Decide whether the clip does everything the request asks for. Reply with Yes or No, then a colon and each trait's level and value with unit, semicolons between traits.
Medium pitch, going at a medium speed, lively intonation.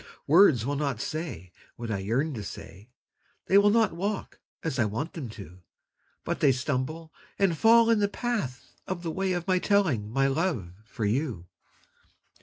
Yes: medium, 150 Hz; average, 175 wpm; wide, 8.3 semitones